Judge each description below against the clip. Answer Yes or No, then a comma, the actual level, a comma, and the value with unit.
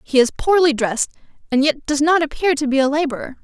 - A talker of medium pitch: No, very high, 290 Hz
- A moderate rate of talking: No, fast, 225 wpm